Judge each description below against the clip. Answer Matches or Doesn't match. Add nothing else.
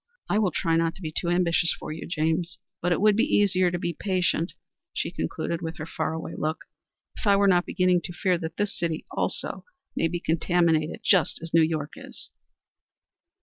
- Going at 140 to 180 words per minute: Doesn't match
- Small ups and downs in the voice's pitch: Matches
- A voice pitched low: Doesn't match